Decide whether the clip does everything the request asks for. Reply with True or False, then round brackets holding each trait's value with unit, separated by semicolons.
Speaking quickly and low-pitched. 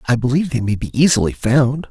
True (220 wpm; 130 Hz)